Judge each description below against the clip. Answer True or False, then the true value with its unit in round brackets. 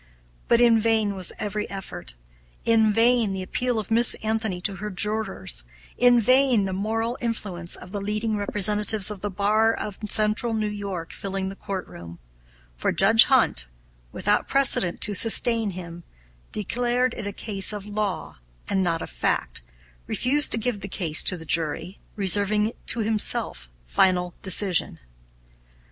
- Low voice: False (205 Hz)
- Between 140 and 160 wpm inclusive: True (155 wpm)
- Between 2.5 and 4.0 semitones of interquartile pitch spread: True (3.1 semitones)